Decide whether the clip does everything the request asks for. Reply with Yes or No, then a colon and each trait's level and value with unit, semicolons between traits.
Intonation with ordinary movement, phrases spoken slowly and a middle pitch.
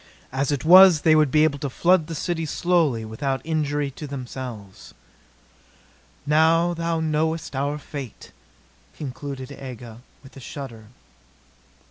Yes: average, 3.4 semitones; slow, 130 wpm; medium, 145 Hz